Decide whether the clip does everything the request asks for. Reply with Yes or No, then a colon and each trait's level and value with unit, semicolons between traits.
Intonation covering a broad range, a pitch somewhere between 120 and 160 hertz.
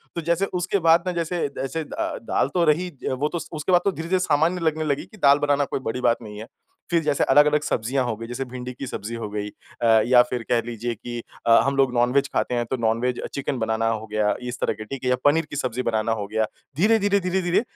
Yes: wide, 5.7 semitones; low, 135 Hz